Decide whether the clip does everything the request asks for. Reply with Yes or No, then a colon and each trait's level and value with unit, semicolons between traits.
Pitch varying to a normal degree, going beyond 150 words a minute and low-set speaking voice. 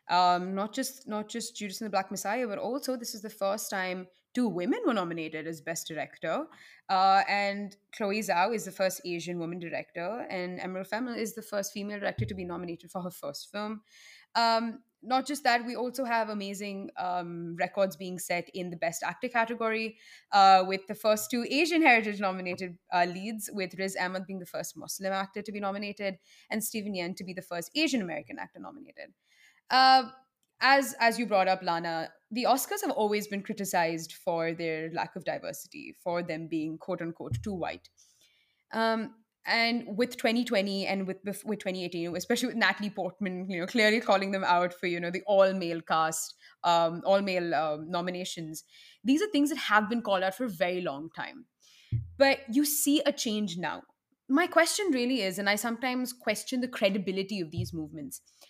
No: average, 4.4 semitones; average, 190 wpm; high, 200 Hz